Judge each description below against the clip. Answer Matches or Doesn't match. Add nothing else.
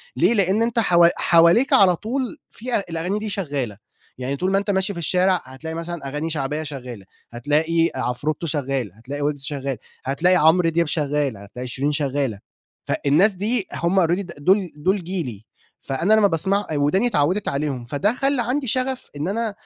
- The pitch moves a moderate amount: Doesn't match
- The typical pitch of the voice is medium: Matches